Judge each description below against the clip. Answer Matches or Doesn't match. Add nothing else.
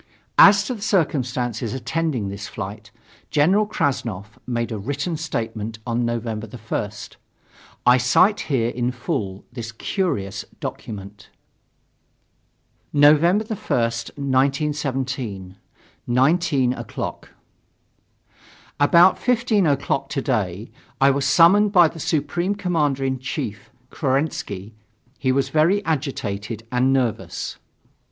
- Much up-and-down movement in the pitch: Matches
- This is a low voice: Matches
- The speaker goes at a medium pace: Doesn't match